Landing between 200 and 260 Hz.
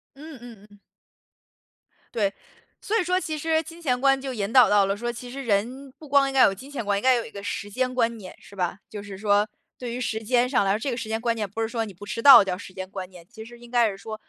Yes: high, 230 Hz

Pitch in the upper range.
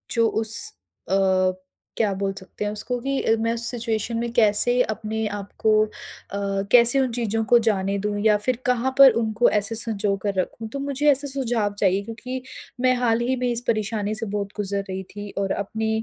Yes: high, 220 Hz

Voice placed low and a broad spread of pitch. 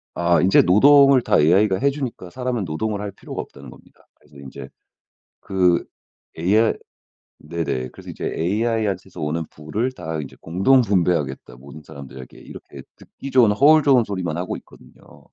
Yes: very low, 95 Hz; wide, 6.5 semitones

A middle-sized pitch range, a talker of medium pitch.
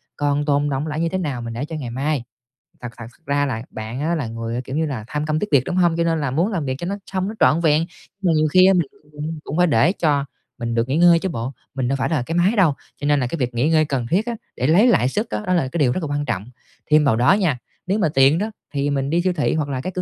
Yes: average, 4.4 semitones; medium, 150 Hz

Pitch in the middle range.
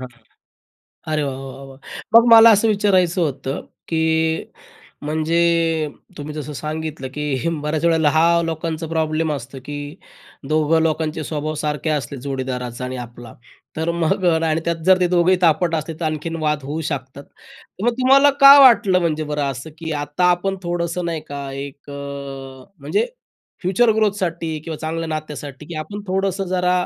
Yes: medium, 160 Hz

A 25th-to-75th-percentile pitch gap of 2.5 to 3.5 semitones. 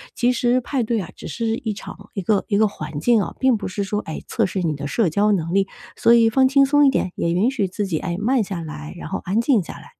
No: average, 4.5 semitones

